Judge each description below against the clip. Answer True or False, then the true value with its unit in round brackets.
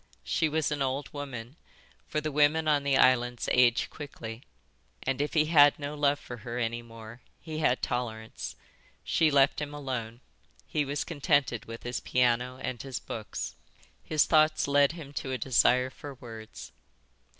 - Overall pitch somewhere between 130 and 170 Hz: True (135 Hz)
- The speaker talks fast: False (165 wpm)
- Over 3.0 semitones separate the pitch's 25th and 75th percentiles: True (3.4 semitones)